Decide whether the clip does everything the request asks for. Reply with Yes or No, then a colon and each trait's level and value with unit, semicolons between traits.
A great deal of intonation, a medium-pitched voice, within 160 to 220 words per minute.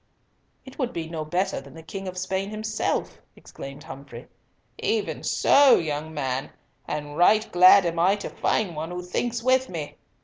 Yes: wide, 5.7 semitones; medium, 180 Hz; average, 170 wpm